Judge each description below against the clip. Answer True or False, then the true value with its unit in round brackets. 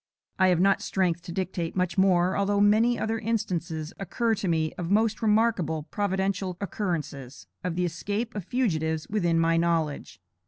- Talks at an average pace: True (160 wpm)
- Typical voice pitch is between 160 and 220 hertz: True (185 Hz)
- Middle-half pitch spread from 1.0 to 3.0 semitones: False (3.7 semitones)